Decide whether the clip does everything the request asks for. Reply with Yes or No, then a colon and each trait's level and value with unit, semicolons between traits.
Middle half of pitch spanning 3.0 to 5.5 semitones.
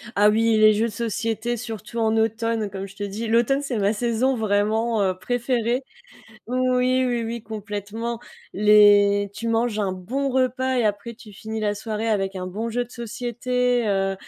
No: narrow, 2.6 semitones